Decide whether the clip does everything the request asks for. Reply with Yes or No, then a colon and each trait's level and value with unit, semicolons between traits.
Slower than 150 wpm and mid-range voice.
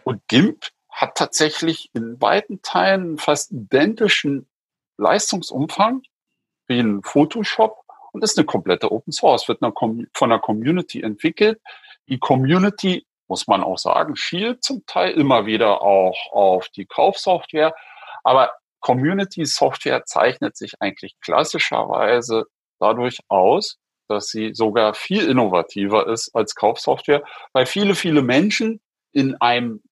Yes: slow, 125 wpm; medium, 155 Hz